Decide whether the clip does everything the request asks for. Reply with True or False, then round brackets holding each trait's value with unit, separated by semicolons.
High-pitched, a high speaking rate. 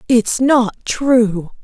False (230 Hz; 110 wpm)